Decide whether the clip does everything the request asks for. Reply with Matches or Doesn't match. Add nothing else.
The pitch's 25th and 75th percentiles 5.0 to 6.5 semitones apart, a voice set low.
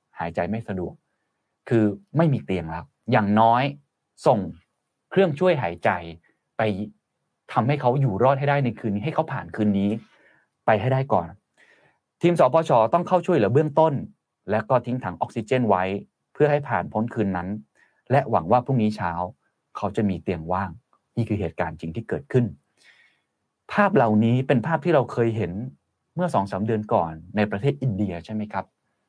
Matches